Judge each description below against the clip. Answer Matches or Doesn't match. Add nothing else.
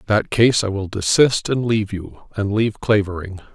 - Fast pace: Doesn't match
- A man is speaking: Matches